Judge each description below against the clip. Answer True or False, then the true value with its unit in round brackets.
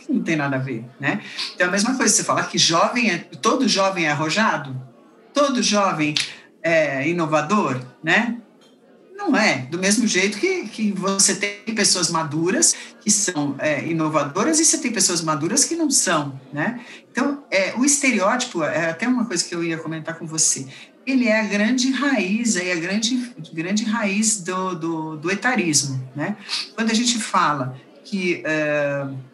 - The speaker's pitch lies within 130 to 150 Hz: False (195 Hz)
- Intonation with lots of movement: True (6.7 semitones)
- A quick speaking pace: False (175 wpm)